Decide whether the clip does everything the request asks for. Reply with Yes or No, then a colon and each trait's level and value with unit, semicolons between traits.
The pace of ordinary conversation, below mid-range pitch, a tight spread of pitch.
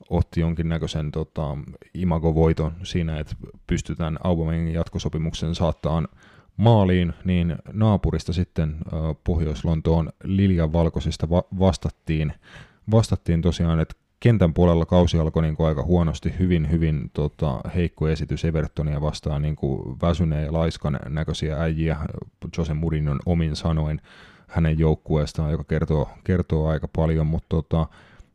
Yes: average, 120 wpm; very low, 80 Hz; narrow, 1.9 semitones